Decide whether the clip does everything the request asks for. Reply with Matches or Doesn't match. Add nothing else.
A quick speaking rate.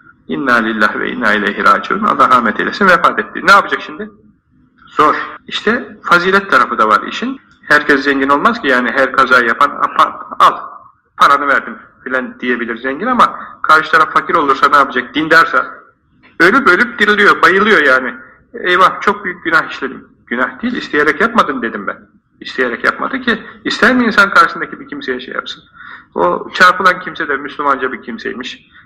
Matches